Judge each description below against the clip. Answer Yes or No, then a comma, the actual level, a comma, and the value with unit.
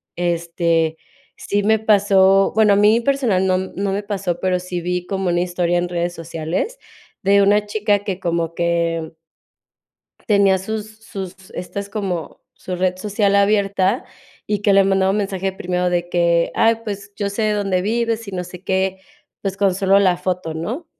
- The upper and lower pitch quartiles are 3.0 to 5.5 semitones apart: No, narrow, 2.4 semitones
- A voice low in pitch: No, high, 190 Hz